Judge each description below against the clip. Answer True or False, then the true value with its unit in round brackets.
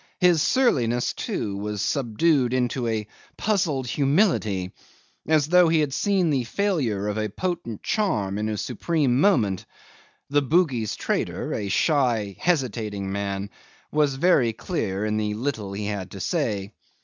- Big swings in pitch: True (7.0 semitones)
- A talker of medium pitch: False (120 Hz)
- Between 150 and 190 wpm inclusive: False (140 wpm)